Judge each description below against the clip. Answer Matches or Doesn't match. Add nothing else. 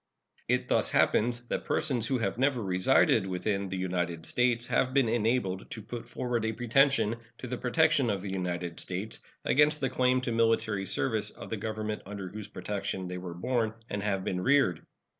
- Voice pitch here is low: Matches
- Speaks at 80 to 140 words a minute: Doesn't match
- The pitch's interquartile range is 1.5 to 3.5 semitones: Doesn't match